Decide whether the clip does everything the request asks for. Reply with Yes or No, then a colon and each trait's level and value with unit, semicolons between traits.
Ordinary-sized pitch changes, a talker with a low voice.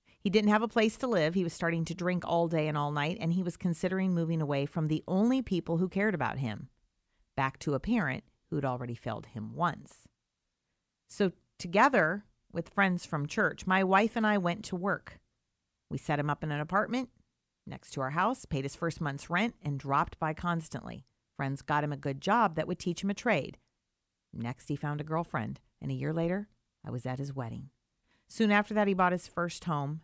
No: average, 4.9 semitones; medium, 170 Hz